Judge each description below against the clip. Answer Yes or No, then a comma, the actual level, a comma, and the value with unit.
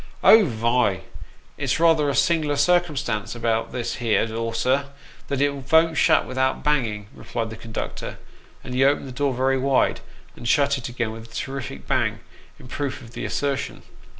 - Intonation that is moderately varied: Yes, average, 3.6 semitones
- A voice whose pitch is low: Yes, low, 130 Hz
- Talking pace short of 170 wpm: No, average, 175 wpm